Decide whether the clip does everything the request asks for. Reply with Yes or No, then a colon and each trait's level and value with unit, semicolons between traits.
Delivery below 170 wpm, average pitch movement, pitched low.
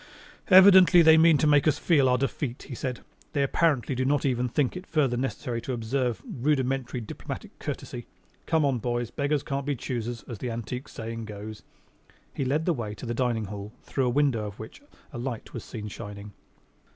No: average, 195 wpm; average, 3.8 semitones; low, 125 Hz